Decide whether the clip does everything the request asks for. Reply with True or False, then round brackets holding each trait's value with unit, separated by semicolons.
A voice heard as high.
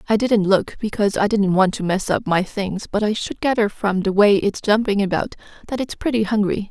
True (205 Hz)